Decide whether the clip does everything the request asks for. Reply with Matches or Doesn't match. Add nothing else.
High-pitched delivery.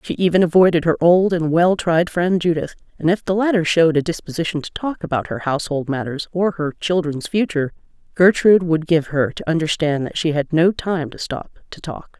Doesn't match